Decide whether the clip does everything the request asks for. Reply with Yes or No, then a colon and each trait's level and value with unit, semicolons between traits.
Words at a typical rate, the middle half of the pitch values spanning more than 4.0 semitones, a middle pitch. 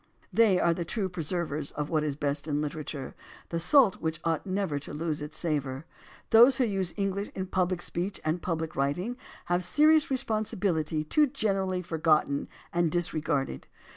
Yes: average, 170 wpm; average, 4.4 semitones; medium, 170 Hz